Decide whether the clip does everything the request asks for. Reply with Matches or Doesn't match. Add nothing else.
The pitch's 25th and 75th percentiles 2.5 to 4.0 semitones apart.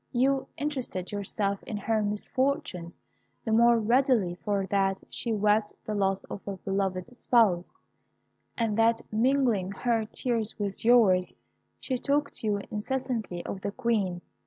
Matches